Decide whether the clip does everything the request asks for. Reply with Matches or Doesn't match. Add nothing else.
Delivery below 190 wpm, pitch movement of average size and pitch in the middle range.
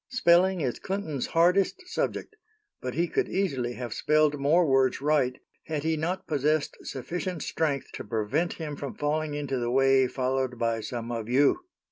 Matches